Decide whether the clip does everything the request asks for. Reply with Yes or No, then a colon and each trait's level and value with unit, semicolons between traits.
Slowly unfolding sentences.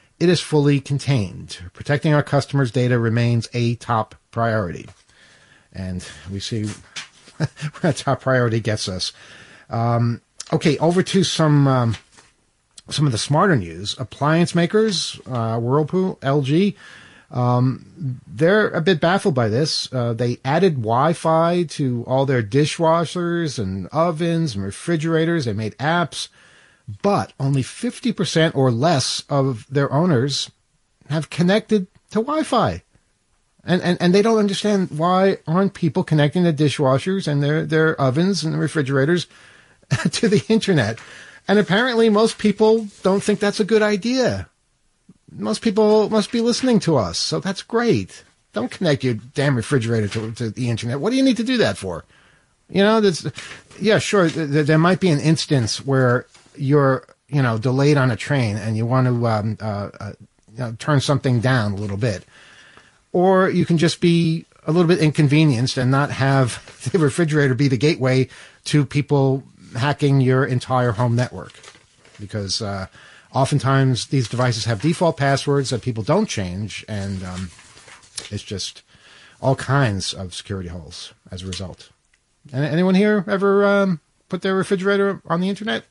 No: average, 155 wpm